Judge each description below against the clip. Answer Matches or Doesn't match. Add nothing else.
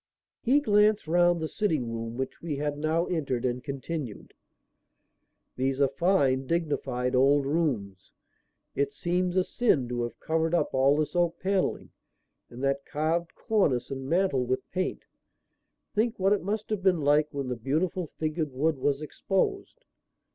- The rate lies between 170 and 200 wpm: Doesn't match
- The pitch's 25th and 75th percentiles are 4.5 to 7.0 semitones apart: Matches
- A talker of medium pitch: Matches